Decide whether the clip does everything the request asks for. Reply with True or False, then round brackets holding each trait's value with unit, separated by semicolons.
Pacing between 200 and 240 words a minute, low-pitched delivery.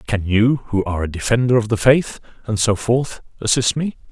True (205 wpm; 115 Hz)